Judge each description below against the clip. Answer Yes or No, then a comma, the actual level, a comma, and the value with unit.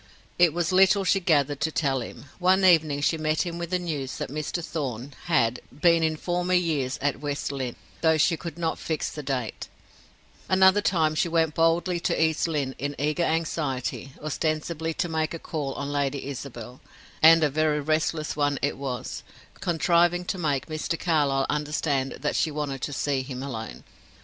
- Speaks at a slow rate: No, average, 180 wpm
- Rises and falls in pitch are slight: No, average, 3.0 semitones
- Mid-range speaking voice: Yes, medium, 155 Hz